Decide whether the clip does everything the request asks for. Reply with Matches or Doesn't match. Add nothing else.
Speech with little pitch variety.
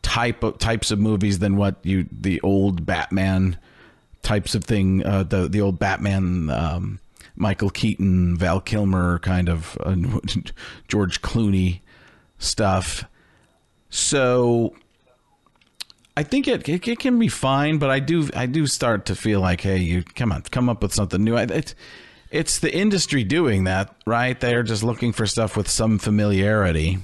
Doesn't match